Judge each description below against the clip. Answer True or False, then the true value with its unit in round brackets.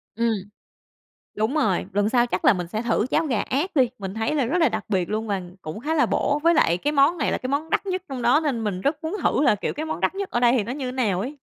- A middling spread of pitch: False (5.8 semitones)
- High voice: True (250 Hz)